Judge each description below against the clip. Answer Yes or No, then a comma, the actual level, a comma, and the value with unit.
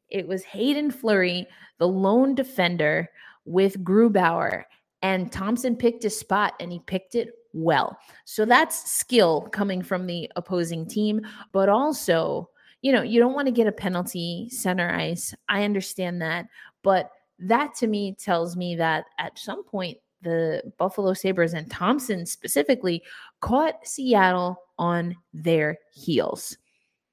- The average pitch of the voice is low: No, high, 190 Hz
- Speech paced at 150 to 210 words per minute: No, average, 140 wpm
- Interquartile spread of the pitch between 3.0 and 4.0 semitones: No, average, 4.6 semitones